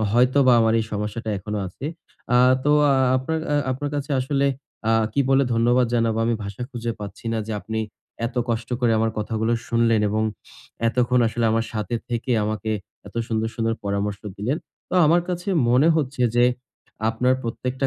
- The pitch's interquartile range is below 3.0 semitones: Yes, narrow, 2.6 semitones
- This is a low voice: Yes, low, 115 Hz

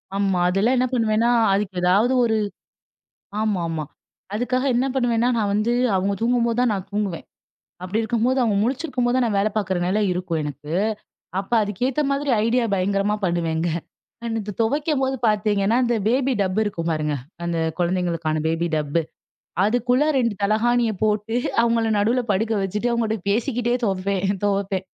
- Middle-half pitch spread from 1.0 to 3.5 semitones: No, average, 4.1 semitones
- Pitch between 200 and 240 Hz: Yes, high, 210 Hz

